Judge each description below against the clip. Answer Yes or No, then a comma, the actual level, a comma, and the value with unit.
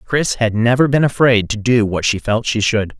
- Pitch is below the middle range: Yes, low, 115 Hz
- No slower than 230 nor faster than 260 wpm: Yes, fast, 240 wpm